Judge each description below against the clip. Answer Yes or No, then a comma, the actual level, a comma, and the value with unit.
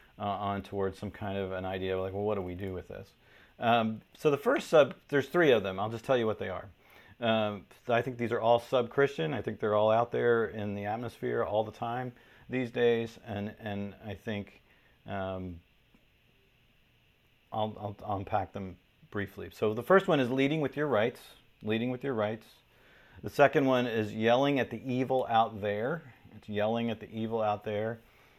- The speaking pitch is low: Yes, low, 110 Hz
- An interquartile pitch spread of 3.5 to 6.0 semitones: No, average, 2.9 semitones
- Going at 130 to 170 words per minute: No, average, 200 wpm